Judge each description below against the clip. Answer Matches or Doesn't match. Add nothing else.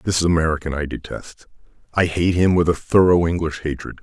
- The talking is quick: Matches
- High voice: Doesn't match